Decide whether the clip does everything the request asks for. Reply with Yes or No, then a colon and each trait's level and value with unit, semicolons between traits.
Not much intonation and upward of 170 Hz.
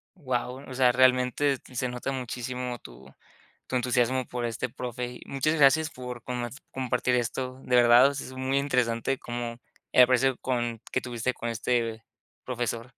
No: narrow, 1.4 semitones; low, 125 Hz